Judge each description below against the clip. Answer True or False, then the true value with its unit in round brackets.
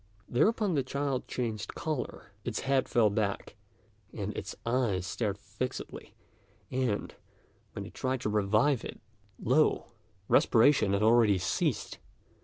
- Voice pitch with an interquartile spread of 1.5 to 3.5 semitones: False (3.9 semitones)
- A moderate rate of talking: False (125 wpm)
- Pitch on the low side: True (120 Hz)